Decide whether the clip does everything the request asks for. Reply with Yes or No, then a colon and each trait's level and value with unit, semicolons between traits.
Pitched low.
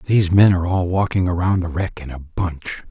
Yes: very low, 90 Hz